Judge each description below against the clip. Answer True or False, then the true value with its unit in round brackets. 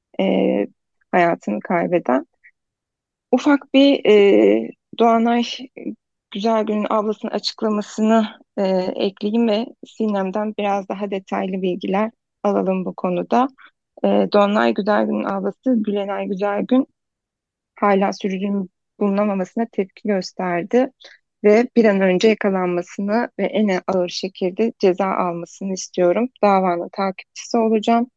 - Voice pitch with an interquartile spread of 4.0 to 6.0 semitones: False (3.0 semitones)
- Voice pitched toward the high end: True (205 Hz)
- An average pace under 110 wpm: True (100 wpm)